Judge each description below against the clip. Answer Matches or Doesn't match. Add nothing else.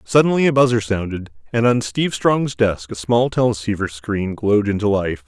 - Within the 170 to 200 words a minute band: Matches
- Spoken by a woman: Doesn't match